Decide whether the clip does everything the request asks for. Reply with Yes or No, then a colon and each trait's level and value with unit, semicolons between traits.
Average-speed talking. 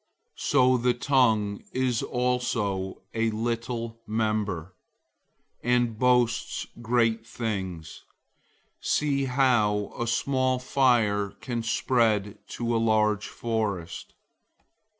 No: slow, 95 wpm